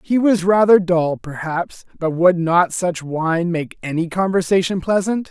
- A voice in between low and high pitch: Yes, medium, 175 Hz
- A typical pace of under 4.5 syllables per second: Yes, 4.2 syllables/s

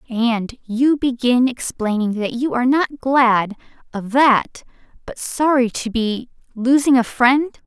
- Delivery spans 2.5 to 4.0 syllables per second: Yes, 3.8 syllables/s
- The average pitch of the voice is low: No, high, 245 Hz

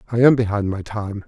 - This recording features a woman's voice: No, male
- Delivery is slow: No, fast, 235 wpm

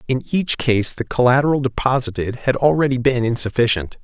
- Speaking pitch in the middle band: No, low, 125 Hz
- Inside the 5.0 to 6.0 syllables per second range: Yes, 5.6 syllables/s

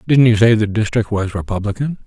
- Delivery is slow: No, fast, 205 wpm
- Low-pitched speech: Yes, low, 110 Hz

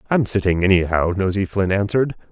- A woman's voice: No, male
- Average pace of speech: Yes, average, 155 wpm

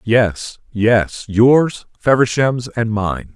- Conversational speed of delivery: No, slow, 90 wpm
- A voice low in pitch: Yes, low, 115 Hz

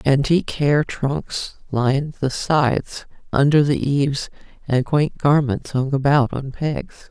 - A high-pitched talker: No, medium, 140 Hz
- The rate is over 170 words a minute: No, slow, 135 wpm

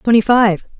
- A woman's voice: Yes, female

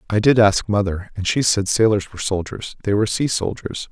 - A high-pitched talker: No, low, 105 Hz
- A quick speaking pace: Yes, fast, 215 wpm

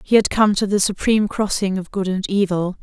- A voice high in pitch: Yes, high, 195 Hz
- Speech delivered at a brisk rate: Yes, fast, 235 wpm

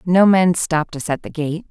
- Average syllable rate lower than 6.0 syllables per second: Yes, 5.0 syllables/s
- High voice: No, medium, 170 Hz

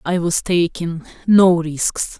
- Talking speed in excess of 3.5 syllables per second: No, 3.3 syllables/s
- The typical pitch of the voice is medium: Yes, medium, 170 Hz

